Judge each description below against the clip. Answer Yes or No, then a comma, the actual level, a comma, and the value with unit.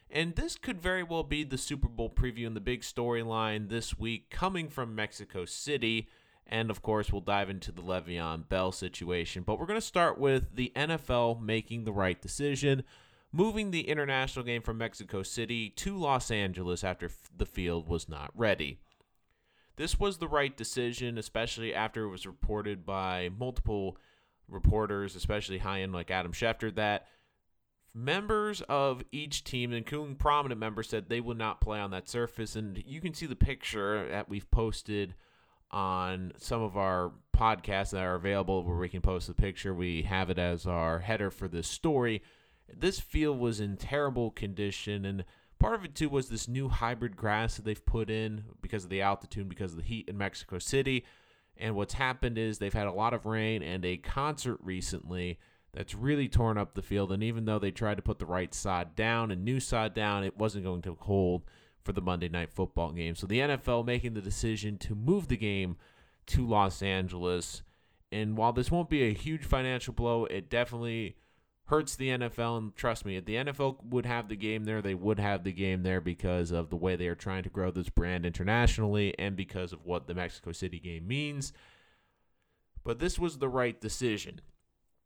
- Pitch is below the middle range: Yes, low, 105 Hz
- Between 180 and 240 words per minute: Yes, average, 195 wpm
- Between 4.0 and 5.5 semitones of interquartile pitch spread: Yes, average, 4.3 semitones